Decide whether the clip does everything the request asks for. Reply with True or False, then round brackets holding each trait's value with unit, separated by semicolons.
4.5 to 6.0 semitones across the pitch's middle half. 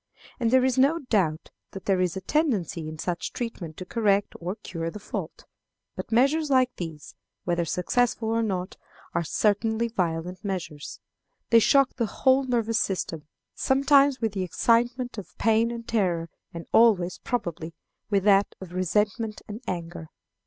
True (5.1 semitones)